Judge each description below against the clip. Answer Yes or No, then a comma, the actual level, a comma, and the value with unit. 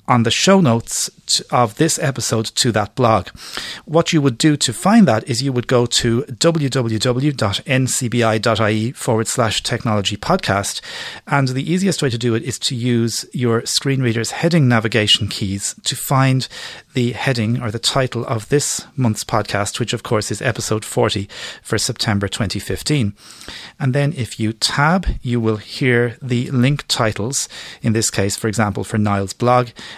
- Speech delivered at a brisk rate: No, average, 165 wpm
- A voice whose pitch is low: Yes, low, 120 Hz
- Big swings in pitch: No, average, 3.3 semitones